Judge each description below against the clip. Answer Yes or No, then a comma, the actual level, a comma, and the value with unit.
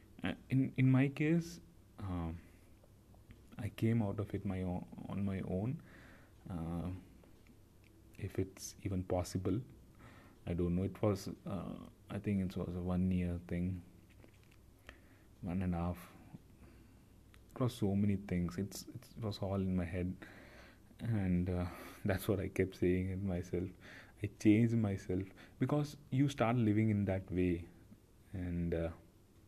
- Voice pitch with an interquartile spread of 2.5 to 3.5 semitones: Yes, average, 3.0 semitones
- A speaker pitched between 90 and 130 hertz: Yes, very low, 95 Hz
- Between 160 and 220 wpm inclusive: No, average, 145 wpm